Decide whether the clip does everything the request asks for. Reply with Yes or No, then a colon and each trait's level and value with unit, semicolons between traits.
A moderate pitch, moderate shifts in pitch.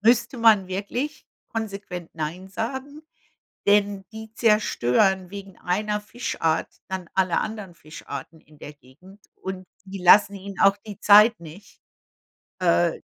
No: high, 195 Hz; average, 3.0 semitones